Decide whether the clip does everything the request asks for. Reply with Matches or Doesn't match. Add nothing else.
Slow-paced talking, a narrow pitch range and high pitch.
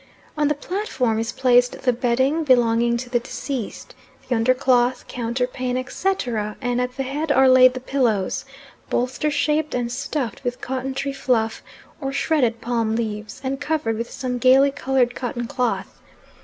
Doesn't match